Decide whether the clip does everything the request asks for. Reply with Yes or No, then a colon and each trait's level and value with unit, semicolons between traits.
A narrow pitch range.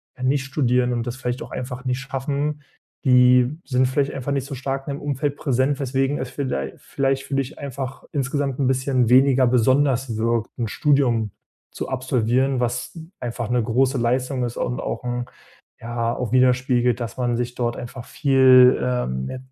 Yes: narrow, 1.9 semitones